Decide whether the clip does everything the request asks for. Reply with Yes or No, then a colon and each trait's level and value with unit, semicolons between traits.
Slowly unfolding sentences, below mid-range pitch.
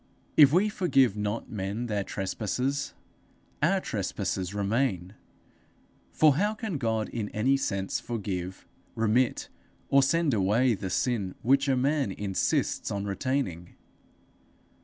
Yes: slow, 120 wpm; low, 115 Hz